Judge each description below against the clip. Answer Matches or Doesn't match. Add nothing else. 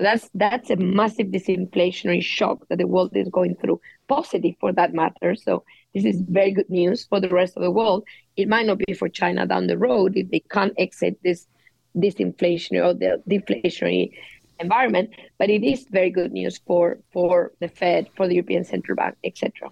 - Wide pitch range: Doesn't match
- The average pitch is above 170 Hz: Matches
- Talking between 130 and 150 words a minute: Doesn't match